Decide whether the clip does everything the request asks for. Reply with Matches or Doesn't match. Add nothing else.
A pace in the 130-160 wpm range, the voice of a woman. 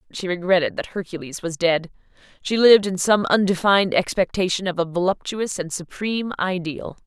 Matches